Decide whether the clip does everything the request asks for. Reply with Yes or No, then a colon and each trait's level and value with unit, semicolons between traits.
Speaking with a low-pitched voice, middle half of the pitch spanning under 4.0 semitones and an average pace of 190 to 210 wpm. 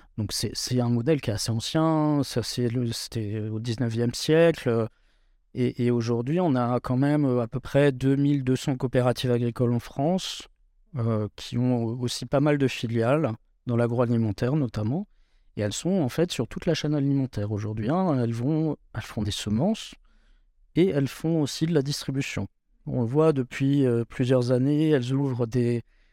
No: low, 125 Hz; average, 3.6 semitones; average, 175 wpm